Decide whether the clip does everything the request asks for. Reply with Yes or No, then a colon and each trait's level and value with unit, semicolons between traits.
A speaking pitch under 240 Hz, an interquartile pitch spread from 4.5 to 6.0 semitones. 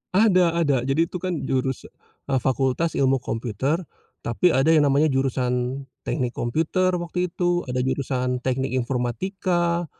Yes: low, 135 Hz; average, 5.0 semitones